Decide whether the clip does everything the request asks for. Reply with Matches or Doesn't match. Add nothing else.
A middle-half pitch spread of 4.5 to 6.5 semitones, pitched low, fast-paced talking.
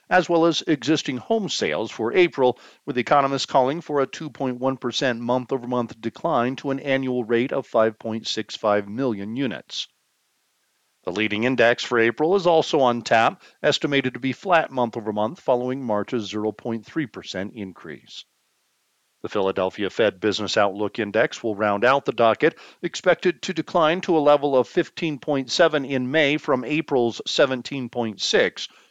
Doesn't match